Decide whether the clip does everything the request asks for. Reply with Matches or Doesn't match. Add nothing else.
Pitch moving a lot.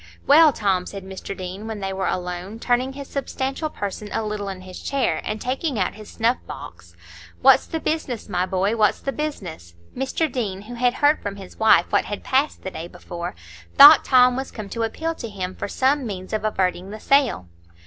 Matches